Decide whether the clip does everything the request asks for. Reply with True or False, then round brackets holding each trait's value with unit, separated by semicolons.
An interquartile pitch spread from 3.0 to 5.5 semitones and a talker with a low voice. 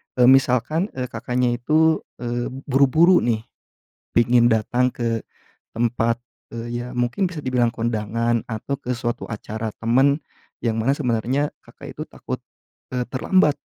False (2.5 semitones; 120 Hz)